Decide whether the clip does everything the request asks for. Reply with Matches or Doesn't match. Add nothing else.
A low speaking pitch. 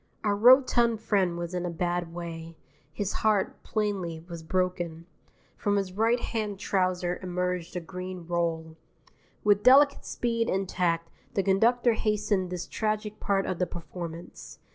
Doesn't match